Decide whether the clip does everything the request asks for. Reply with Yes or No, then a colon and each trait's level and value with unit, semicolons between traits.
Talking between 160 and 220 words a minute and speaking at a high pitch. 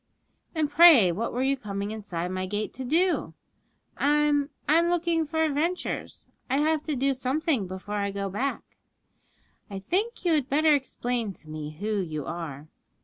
Yes: average, 165 wpm; very high, 260 Hz